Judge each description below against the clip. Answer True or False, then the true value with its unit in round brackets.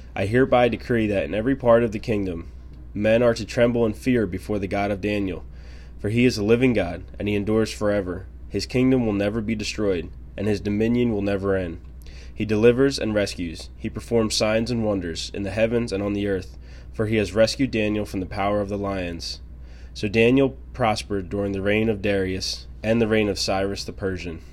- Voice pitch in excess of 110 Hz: False (105 Hz)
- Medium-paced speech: False (210 wpm)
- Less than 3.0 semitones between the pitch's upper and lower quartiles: False (3.4 semitones)